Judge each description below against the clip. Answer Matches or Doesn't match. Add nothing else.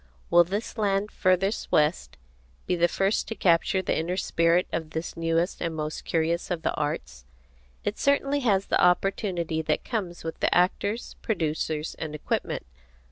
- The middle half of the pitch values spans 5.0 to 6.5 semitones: Doesn't match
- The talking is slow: Doesn't match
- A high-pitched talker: Doesn't match